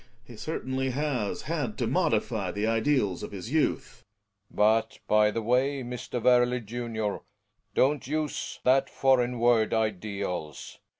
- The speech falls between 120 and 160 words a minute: Yes, average, 145 wpm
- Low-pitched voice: Yes, low, 120 Hz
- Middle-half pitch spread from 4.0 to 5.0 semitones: No, average, 3.4 semitones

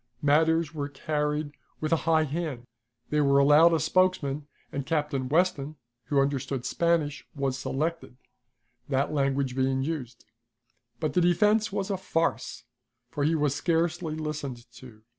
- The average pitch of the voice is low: No, medium, 150 Hz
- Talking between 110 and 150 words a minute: Yes, average, 140 wpm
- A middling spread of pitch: Yes, average, 3.0 semitones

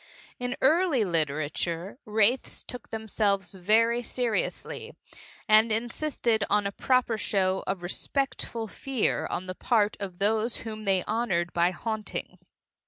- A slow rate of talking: Yes, slow, 125 wpm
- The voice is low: No, high, 215 Hz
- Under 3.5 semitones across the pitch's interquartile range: No, average, 3.8 semitones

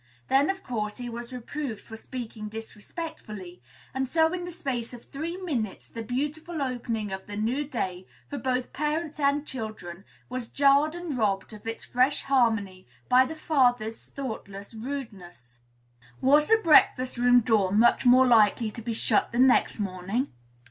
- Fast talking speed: No, average, 160 wpm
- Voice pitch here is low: No, high, 245 Hz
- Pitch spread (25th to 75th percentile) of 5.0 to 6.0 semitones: No, average, 4.6 semitones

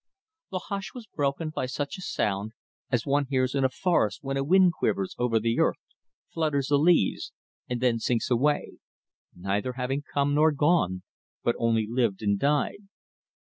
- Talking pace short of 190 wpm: Yes, average, 170 wpm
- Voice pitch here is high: No, low, 135 Hz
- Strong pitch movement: No, average, 4.5 semitones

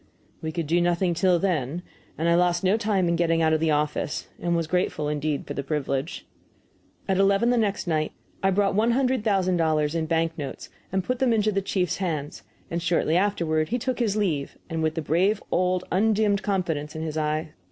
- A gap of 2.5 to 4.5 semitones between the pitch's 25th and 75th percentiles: Yes, average, 3.9 semitones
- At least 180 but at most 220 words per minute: Yes, fast, 205 wpm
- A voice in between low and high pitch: Yes, medium, 175 Hz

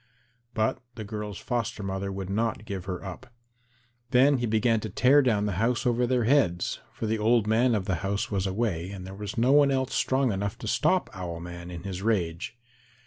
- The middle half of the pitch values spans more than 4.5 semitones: No, average, 3.9 semitones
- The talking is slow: No, fast, 205 wpm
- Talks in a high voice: No, low, 105 Hz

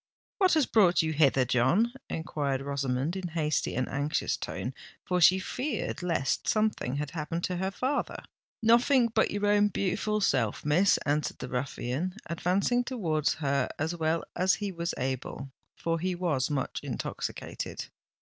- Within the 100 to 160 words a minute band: Yes, average, 145 wpm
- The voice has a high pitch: No, medium, 170 Hz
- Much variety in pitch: Yes, wide, 6.0 semitones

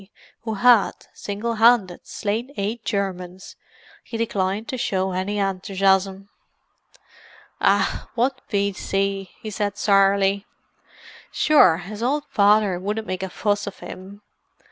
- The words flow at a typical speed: No, slow, 120 wpm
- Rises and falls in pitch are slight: Yes, narrow, 2.2 semitones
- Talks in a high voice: Yes, high, 200 Hz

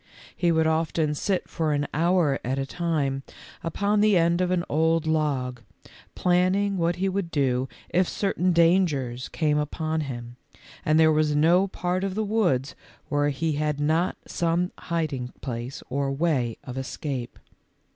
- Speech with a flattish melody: No, average, 4.2 semitones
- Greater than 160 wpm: No, average, 155 wpm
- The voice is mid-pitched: Yes, medium, 160 Hz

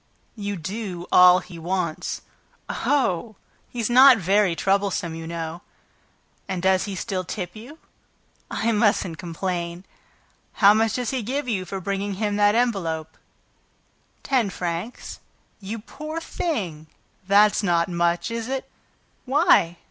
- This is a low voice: No, high, 200 Hz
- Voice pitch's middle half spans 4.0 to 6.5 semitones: Yes, average, 4.6 semitones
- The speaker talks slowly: Yes, slow, 130 wpm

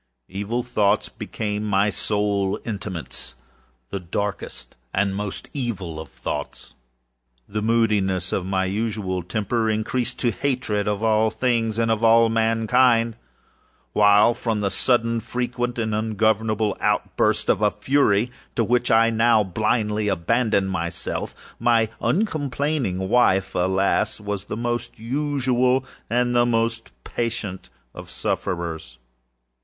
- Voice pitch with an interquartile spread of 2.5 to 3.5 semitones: Yes, average, 3.0 semitones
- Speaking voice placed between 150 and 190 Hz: No, low, 110 Hz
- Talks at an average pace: No, slow, 120 wpm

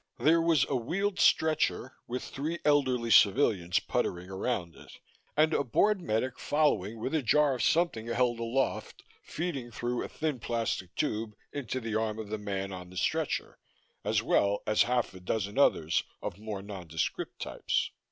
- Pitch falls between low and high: No, low, 120 Hz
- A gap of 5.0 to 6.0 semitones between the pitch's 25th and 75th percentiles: Yes, wide, 5.6 semitones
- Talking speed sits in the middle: Yes, average, 165 wpm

